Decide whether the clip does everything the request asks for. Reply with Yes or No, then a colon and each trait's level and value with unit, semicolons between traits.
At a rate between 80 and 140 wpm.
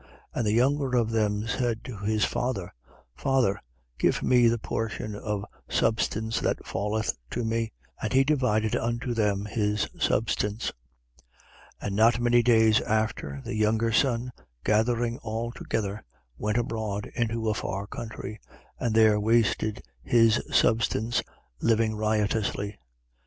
Yes: slow, 135 wpm